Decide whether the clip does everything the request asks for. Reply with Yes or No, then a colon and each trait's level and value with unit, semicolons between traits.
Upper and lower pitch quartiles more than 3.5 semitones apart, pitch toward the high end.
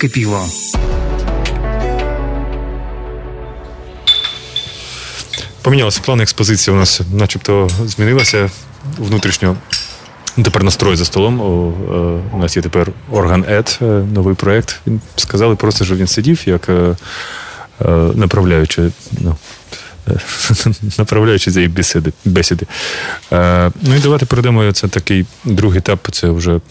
No: average, 3.9 semitones; low, 100 Hz